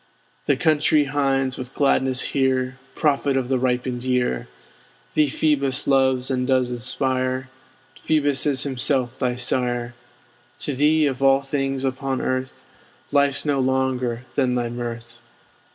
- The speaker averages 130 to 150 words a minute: Yes, slow, 135 wpm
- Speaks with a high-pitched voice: No, low, 130 Hz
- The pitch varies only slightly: Yes, narrow, 1.6 semitones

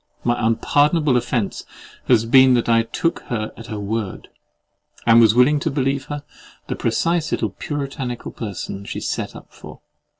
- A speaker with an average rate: Yes, average, 160 wpm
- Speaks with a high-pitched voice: No, low, 125 Hz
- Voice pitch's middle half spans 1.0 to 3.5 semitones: No, average, 4.1 semitones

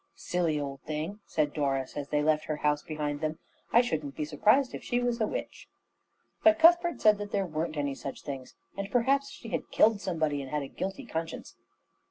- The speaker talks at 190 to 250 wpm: Yes, fast, 205 wpm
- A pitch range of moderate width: No, wide, 6.5 semitones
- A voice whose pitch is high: No, medium, 160 Hz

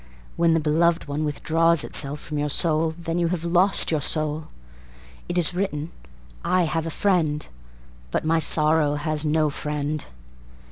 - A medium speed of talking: Yes, average, 155 wpm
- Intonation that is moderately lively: No, narrow, 2.0 semitones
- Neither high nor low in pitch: Yes, medium, 155 Hz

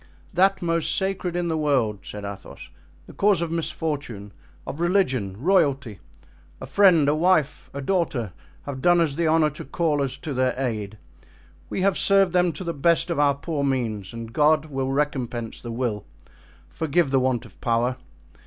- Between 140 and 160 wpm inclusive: No, average, 175 wpm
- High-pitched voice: No, medium, 145 Hz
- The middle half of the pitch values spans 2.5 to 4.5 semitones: No, average, 5.3 semitones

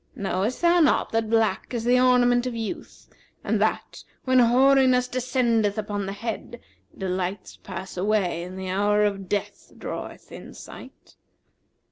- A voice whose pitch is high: Yes, high, 220 Hz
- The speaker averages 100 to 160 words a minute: Yes, average, 145 wpm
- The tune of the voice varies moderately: Yes, average, 4.2 semitones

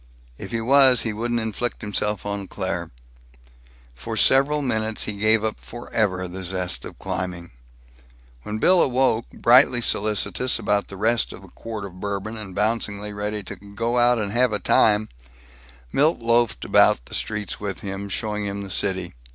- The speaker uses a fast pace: No, average, 165 wpm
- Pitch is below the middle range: Yes, low, 105 Hz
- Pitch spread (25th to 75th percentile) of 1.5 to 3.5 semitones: Yes, average, 2.7 semitones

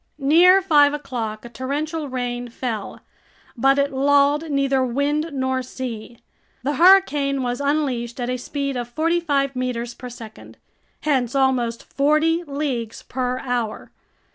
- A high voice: Yes, very high, 270 Hz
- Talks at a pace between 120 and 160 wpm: Yes, average, 140 wpm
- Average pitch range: Yes, average, 3.0 semitones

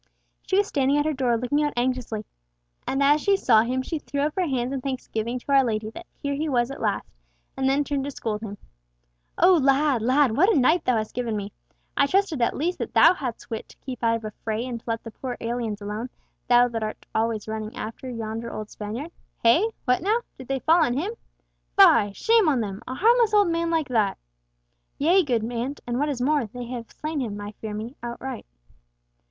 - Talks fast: Yes, fast, 220 wpm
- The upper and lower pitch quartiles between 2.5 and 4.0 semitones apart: No, average, 4.5 semitones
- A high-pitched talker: Yes, very high, 255 Hz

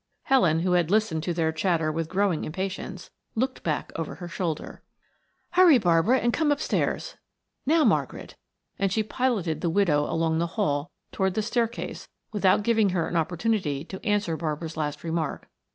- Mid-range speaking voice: Yes, medium, 180 Hz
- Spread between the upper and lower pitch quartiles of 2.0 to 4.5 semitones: No, average, 5.0 semitones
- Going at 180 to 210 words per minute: No, average, 165 wpm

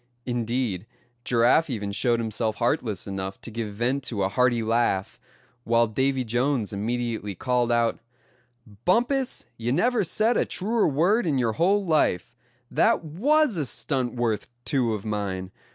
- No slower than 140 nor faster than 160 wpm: Yes, average, 150 wpm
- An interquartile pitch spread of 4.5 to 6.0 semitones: Yes, average, 5.2 semitones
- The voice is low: Yes, low, 120 Hz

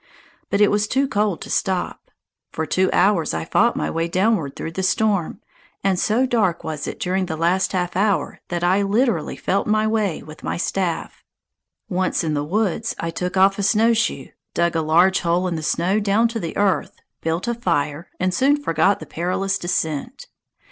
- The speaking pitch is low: No, medium, 185 Hz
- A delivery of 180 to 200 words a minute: Yes, average, 190 wpm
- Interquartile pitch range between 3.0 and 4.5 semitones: Yes, average, 3.8 semitones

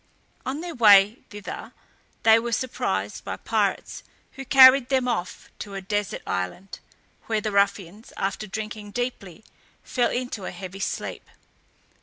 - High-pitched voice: Yes, high, 215 Hz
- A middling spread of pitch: Yes, average, 3.8 semitones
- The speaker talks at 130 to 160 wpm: Yes, average, 140 wpm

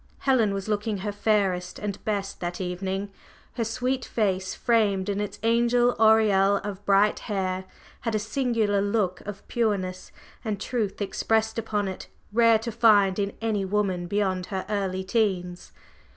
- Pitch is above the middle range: Yes, high, 205 Hz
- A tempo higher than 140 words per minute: Yes, average, 150 wpm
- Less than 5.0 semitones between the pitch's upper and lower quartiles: Yes, narrow, 2.5 semitones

